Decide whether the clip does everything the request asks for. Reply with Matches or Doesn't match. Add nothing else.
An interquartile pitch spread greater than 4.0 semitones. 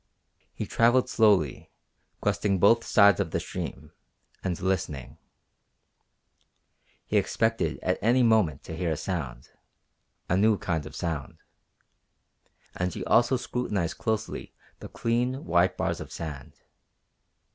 Matches